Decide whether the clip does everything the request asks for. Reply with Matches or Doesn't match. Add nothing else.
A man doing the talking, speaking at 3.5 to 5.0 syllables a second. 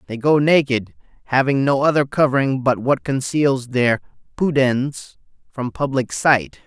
Matches